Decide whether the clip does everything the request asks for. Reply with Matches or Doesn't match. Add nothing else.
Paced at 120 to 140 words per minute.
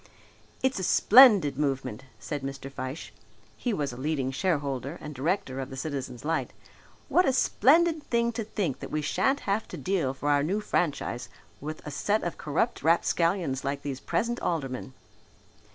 Doesn't match